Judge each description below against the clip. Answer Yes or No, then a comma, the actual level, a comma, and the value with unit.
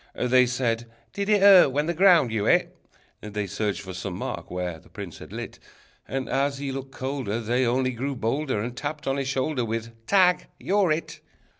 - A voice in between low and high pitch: No, low, 130 Hz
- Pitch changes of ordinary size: Yes, average, 4.4 semitones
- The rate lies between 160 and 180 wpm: No, average, 195 wpm